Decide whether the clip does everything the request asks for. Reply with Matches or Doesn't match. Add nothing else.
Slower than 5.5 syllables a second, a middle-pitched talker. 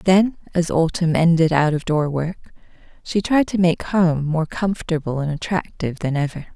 Matches